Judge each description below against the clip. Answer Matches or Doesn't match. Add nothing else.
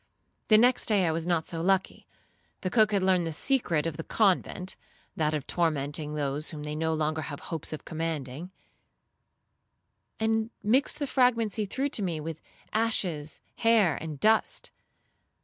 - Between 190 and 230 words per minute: Doesn't match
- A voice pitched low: Doesn't match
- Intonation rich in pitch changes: Matches